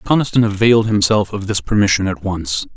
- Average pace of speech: Yes, average, 175 wpm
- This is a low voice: Yes, low, 100 Hz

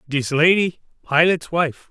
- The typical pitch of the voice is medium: Yes, medium, 160 Hz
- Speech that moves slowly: Yes, slow, 125 wpm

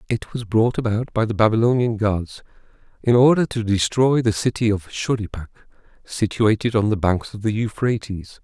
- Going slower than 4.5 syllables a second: No, 5.1 syllables/s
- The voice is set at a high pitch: No, low, 110 Hz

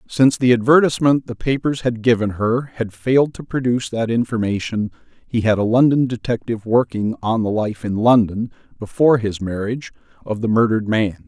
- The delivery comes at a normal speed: Yes, average, 170 wpm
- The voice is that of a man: Yes, male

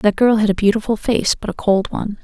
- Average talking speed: No, fast, 270 wpm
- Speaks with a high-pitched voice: Yes, high, 215 Hz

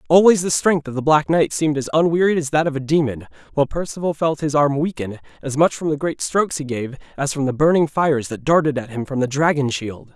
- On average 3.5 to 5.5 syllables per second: No, 6.1 syllables/s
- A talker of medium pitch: Yes, medium, 150 Hz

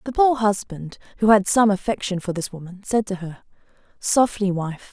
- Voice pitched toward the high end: Yes, high, 200 Hz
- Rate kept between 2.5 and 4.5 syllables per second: No, 5.0 syllables/s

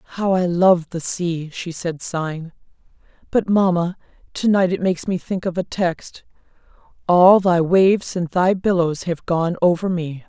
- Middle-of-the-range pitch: Yes, medium, 175 Hz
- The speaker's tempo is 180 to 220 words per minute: No, average, 165 wpm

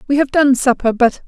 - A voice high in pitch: Yes, very high, 265 Hz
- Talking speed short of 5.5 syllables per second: No, 5.6 syllables/s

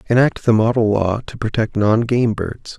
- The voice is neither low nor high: No, low, 110 Hz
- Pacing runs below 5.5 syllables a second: Yes, 4.6 syllables/s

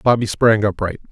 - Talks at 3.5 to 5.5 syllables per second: Yes, 5.4 syllables/s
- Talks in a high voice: No, low, 110 Hz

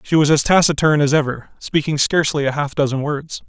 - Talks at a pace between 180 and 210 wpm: Yes, fast, 205 wpm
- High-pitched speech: No, medium, 145 Hz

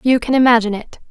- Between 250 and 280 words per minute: No, fast, 215 wpm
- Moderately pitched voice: No, high, 235 Hz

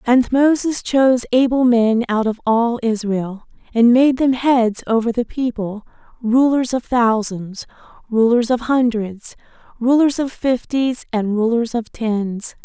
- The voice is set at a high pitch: Yes, high, 235 Hz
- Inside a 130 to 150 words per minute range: Yes, average, 140 wpm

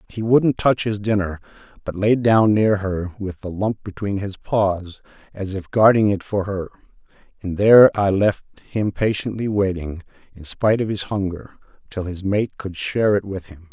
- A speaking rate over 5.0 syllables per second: No, 4.7 syllables/s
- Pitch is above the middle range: No, low, 100 Hz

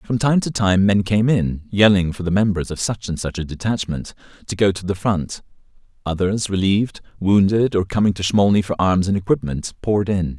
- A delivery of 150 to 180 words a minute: No, average, 200 wpm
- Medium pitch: No, low, 100 Hz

